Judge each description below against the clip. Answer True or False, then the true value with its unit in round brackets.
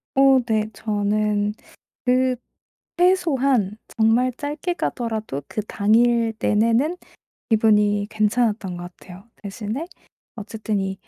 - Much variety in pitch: False (3.4 semitones)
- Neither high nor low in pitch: False (220 Hz)